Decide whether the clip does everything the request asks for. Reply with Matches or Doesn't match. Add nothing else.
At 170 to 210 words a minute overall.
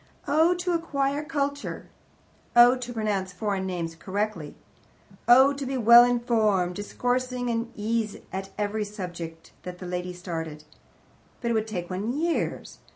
Doesn't match